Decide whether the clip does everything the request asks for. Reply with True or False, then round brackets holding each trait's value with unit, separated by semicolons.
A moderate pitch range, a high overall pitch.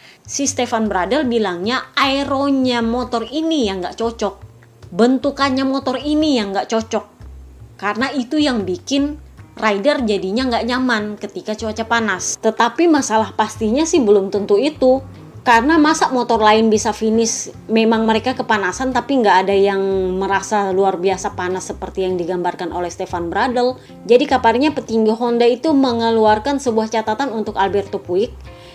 True (4.4 semitones; 225 Hz)